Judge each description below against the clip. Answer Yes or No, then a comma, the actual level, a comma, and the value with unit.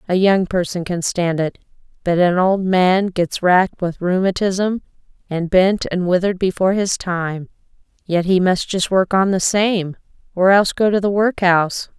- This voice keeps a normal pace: Yes, average, 175 wpm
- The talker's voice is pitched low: No, medium, 185 Hz